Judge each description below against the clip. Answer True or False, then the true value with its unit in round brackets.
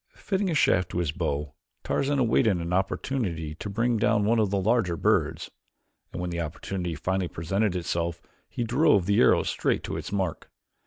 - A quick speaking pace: False (180 wpm)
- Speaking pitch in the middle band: False (95 Hz)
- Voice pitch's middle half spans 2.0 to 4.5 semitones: False (5.1 semitones)